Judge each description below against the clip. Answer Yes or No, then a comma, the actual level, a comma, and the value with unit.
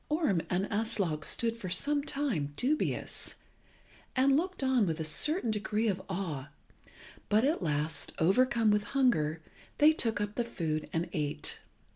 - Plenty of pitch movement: Yes, wide, 8.1 semitones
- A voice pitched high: Yes, high, 210 Hz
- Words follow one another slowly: No, average, 150 wpm